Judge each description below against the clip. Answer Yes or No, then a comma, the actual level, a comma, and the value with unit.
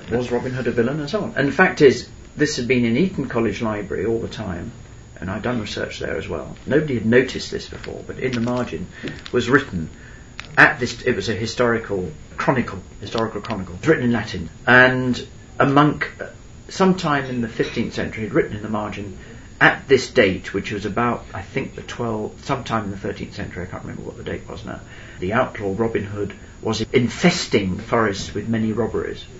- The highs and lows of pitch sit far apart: No, average, 3.4 semitones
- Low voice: Yes, low, 115 Hz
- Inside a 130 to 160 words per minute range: No, fast, 205 wpm